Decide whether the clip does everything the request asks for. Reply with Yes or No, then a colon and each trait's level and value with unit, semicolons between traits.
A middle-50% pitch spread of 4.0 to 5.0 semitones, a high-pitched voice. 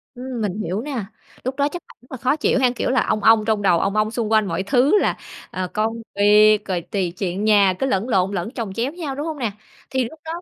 Yes: average, 4.5 semitones; high, 220 Hz